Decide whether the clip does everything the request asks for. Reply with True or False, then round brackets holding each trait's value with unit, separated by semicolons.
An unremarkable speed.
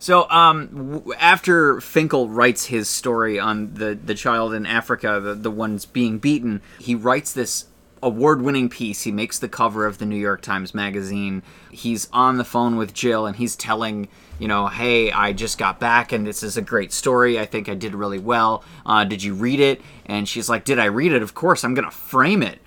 False (215 wpm)